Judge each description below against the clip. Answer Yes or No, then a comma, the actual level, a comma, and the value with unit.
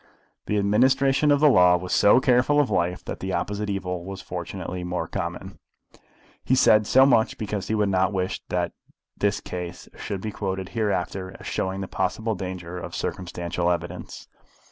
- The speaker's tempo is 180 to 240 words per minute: No, average, 170 wpm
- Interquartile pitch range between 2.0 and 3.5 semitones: Yes, average, 3.2 semitones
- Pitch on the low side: Yes, very low, 95 Hz